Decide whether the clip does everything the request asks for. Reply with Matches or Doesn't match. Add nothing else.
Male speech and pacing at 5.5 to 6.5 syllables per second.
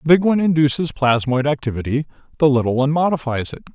Doesn't match